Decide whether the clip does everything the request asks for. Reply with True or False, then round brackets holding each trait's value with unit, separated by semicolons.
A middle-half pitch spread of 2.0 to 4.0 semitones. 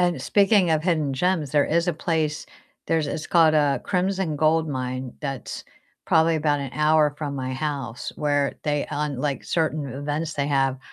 True (2.4 semitones)